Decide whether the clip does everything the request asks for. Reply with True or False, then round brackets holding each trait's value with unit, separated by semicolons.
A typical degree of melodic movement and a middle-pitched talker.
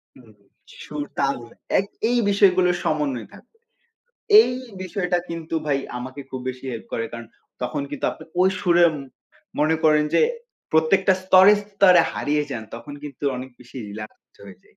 False (6.1 semitones; 150 Hz)